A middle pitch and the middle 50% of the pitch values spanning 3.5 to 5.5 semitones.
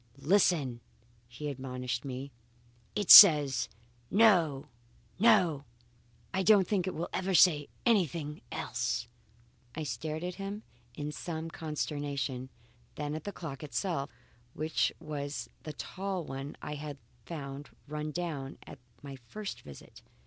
Yes: medium, 150 Hz; average, 4.4 semitones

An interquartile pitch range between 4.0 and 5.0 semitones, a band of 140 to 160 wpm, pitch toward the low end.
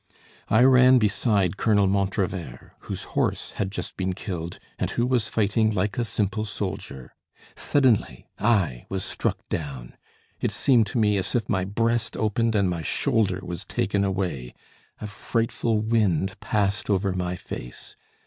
No: average, 3.2 semitones; average, 150 wpm; low, 100 Hz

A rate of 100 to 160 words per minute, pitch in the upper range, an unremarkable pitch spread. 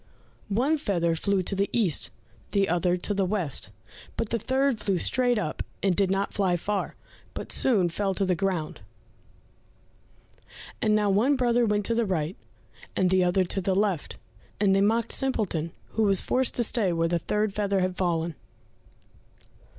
No: average, 175 wpm; high, 195 Hz; average, 3.2 semitones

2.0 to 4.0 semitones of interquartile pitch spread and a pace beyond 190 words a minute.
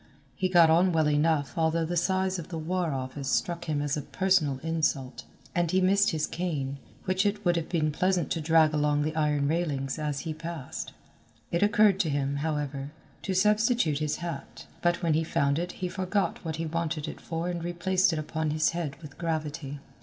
Yes: average, 3.0 semitones; average, 200 wpm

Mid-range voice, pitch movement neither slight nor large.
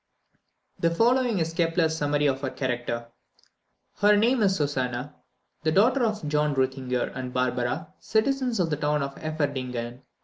No: medium, 150 Hz; wide, 6.8 semitones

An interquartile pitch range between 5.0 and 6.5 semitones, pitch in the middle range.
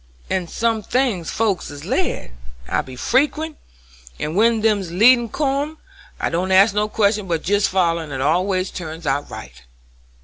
No: wide, 5.4 semitones; high, 195 Hz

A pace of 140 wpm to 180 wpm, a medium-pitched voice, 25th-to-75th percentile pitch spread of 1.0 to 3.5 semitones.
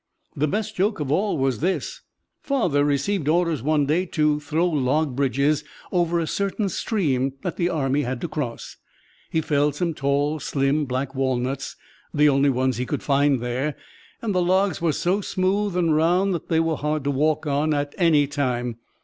No: average, 175 wpm; medium, 150 Hz; average, 3.9 semitones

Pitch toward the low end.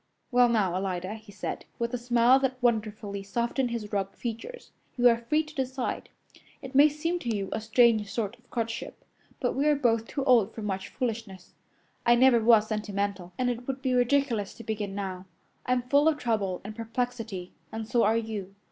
No: high, 230 Hz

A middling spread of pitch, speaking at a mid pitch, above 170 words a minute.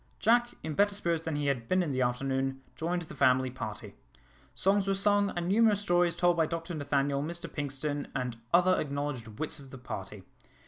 Yes: average, 4.8 semitones; medium, 160 Hz; average, 190 wpm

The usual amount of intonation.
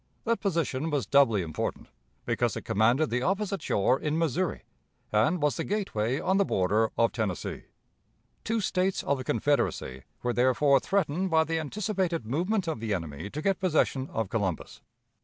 No: wide, 8.3 semitones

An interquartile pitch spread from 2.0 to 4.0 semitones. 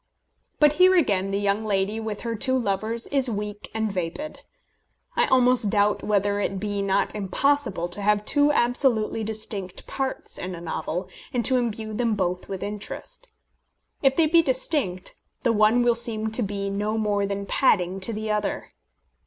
Yes: average, 3.7 semitones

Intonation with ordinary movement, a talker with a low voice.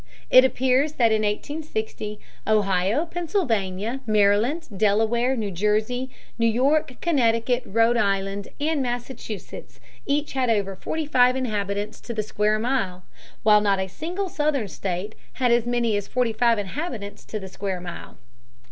No: average, 4.2 semitones; high, 225 Hz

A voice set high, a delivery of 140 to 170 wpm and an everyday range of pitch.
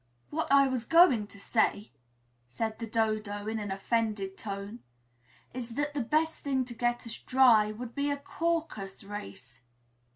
Yes: high, 230 Hz; average, 160 wpm; average, 4.5 semitones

